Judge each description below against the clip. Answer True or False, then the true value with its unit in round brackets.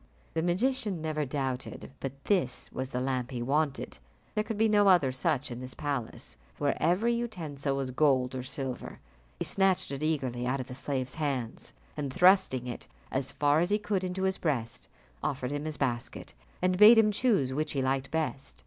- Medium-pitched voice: True (145 Hz)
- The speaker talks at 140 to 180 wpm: False (190 wpm)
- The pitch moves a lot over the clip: True (5.8 semitones)